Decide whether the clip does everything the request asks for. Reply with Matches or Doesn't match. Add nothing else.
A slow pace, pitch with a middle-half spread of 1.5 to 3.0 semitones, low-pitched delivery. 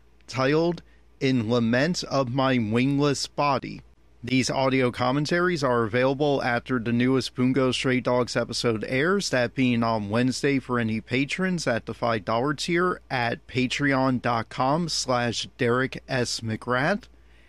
Matches